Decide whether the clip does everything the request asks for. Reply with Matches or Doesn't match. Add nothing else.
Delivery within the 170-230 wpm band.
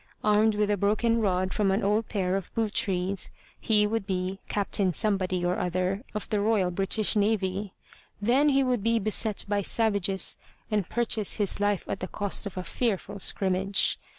Matches